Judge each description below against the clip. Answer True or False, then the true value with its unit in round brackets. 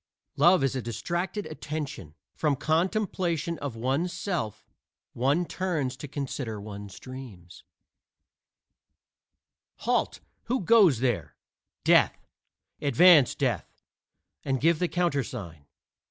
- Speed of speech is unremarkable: False (100 wpm)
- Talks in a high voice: False (140 Hz)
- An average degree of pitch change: False (6.0 semitones)